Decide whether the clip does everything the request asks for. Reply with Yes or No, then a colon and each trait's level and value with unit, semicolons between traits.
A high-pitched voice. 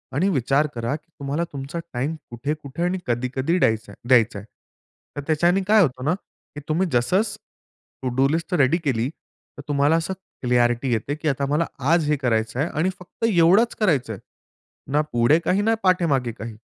No: medium, 145 Hz